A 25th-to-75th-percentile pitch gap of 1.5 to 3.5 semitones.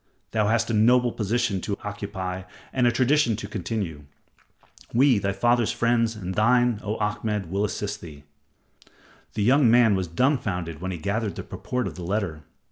No: average, 3.9 semitones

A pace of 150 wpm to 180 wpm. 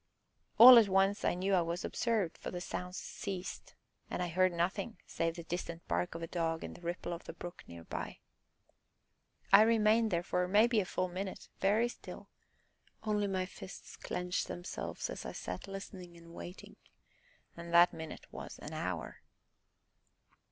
Yes: average, 170 wpm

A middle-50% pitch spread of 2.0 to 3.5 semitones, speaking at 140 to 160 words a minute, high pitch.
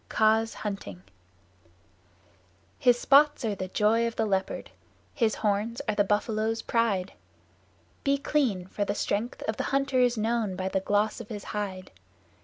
Yes: narrow, 2.6 semitones; average, 155 wpm; high, 215 Hz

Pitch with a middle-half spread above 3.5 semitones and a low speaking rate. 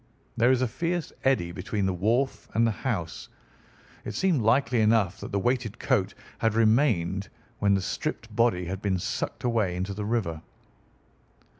No: average, 4.1 semitones; average, 165 wpm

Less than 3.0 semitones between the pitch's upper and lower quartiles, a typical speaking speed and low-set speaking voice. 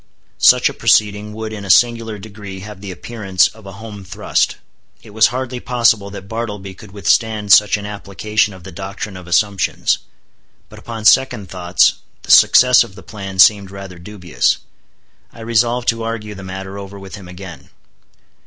Yes: narrow, 2.5 semitones; average, 170 wpm; low, 100 Hz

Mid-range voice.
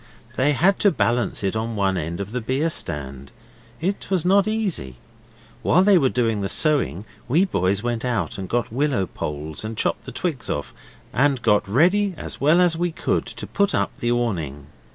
No: low, 120 Hz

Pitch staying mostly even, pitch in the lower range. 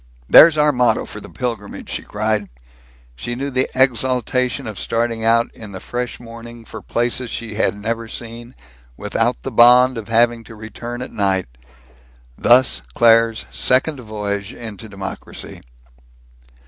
Yes: narrow, 2.3 semitones; low, 115 Hz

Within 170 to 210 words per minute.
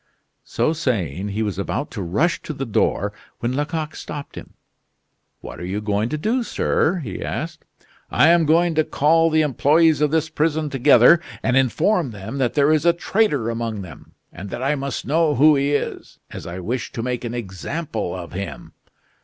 Yes: average, 195 wpm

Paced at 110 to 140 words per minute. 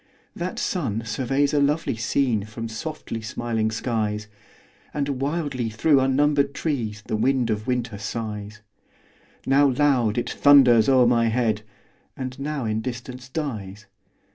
Yes: slow, 135 wpm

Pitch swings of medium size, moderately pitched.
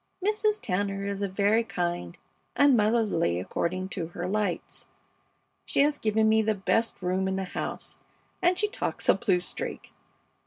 No: average, 3.7 semitones; high, 200 Hz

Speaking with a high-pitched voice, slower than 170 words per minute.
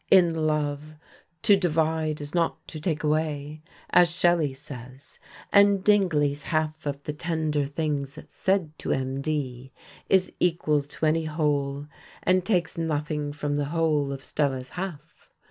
No: medium, 155 Hz; average, 140 wpm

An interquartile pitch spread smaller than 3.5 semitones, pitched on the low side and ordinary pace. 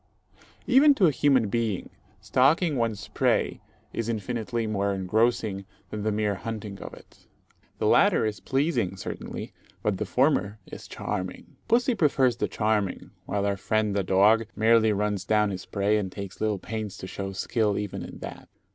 Yes: average, 2.8 semitones; low, 105 Hz; average, 165 wpm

